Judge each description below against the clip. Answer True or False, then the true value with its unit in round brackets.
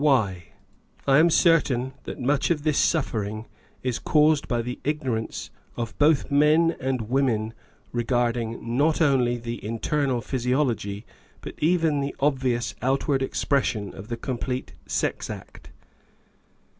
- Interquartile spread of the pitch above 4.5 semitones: False (3.8 semitones)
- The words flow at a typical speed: False (130 wpm)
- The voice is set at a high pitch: False (130 Hz)